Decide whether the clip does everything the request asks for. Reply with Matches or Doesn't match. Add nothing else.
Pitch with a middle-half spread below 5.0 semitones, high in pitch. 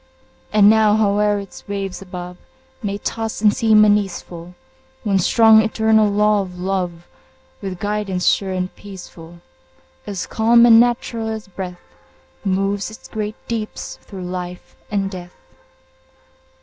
Matches